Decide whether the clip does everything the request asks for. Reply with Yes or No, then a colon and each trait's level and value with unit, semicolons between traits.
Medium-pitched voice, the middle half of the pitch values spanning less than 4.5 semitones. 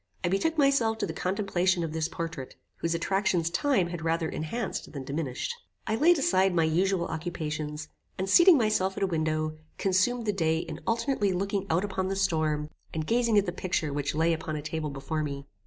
Yes: medium, 175 Hz; average, 4.0 semitones